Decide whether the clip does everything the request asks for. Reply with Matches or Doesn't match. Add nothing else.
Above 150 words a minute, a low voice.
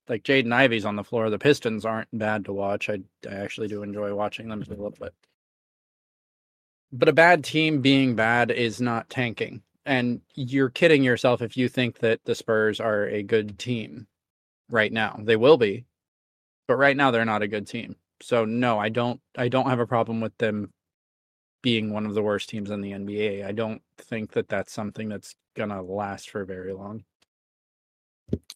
Matches